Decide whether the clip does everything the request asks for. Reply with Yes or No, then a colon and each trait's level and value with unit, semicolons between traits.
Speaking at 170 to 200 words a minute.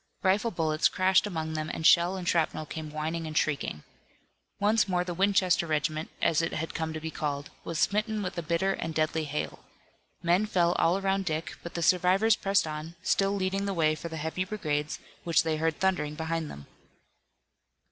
Yes: average, 190 wpm